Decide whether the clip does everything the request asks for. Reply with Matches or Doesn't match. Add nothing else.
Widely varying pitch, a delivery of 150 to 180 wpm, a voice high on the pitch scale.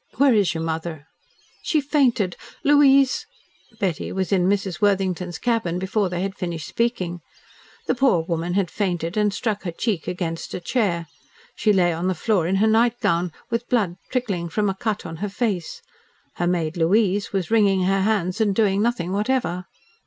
Doesn't match